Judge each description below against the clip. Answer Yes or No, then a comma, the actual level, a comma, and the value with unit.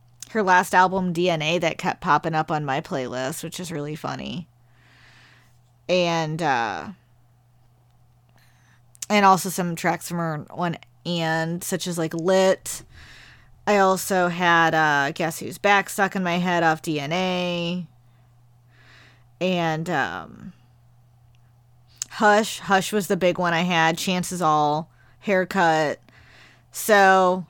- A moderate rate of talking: No, slow, 125 wpm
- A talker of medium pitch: Yes, medium, 165 Hz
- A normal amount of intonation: No, wide, 6.8 semitones